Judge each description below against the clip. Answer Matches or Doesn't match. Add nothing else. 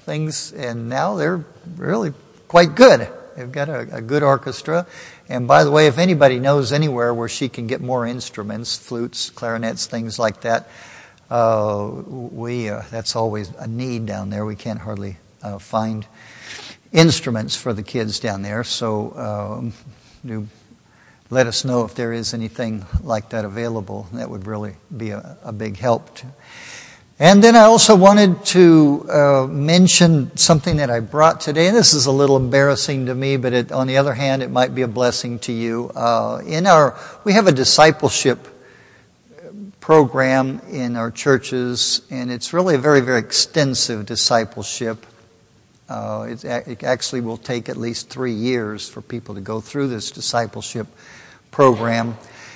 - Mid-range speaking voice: Doesn't match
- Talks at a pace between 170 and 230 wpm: Doesn't match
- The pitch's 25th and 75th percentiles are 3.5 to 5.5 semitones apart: Matches